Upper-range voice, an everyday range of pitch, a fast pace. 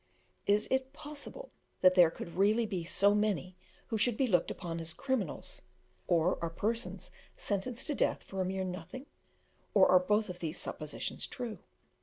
No: high, 200 Hz; average, 4.6 semitones; average, 165 wpm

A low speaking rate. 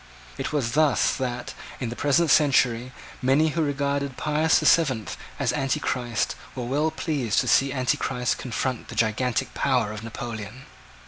No: average, 150 wpm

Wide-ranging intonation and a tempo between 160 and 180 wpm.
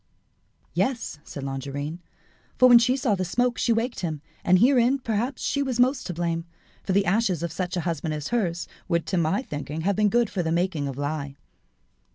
No: wide, 6.8 semitones; fast, 205 wpm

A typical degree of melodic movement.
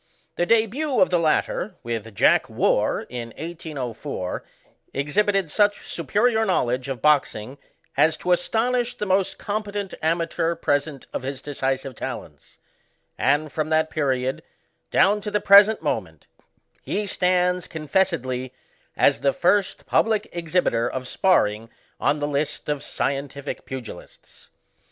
No: wide, 6.6 semitones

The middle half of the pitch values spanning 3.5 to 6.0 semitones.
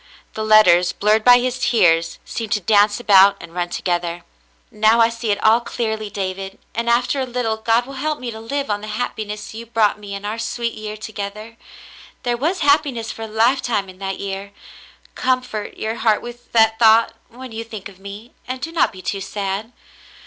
No: average, 2.9 semitones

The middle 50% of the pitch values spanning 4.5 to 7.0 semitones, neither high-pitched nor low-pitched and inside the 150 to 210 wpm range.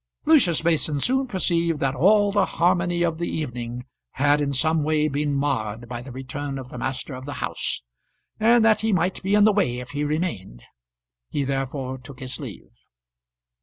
Yes: average, 5.1 semitones; medium, 145 Hz; average, 185 wpm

